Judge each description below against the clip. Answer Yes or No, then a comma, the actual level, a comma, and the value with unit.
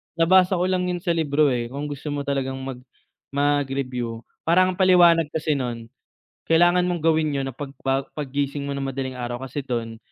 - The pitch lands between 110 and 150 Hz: Yes, medium, 140 Hz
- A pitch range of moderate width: Yes, average, 3.8 semitones